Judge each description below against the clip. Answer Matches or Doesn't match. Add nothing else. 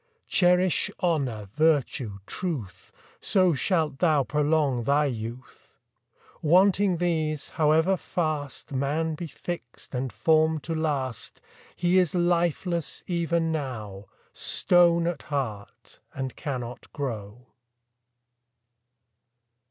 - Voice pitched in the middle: Matches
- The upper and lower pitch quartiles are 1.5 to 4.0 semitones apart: Doesn't match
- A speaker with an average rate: Doesn't match